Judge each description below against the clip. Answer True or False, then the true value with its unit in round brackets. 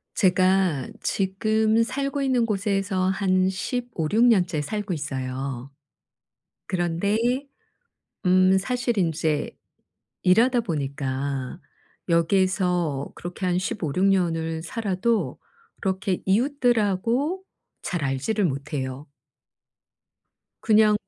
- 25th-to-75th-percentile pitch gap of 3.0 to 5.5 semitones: True (5.2 semitones)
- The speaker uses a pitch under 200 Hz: True (185 Hz)